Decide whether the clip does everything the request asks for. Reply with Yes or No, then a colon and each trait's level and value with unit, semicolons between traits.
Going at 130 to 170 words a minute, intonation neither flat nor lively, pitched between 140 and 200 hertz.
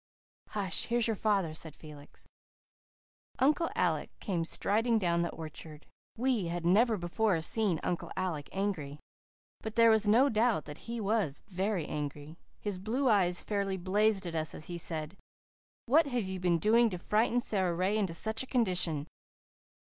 Yes: average, 160 wpm; average, 4.7 semitones; high, 190 Hz